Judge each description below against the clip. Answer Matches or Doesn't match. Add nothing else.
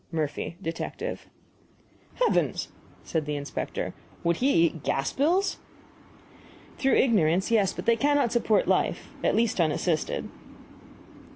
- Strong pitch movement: Matches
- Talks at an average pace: Doesn't match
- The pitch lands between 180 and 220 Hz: Matches